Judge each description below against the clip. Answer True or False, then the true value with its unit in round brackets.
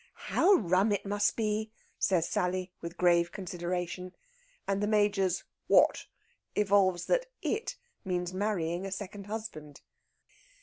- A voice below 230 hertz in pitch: True (190 Hz)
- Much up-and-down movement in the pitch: False (2.7 semitones)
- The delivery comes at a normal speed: False (125 wpm)